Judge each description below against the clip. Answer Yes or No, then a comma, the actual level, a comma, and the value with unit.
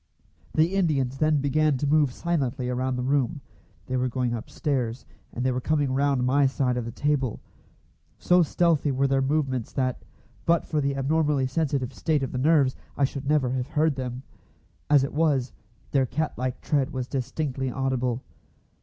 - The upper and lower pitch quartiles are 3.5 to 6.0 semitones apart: No, average, 2.7 semitones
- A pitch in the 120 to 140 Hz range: Yes, low, 135 Hz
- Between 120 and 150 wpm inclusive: No, average, 175 wpm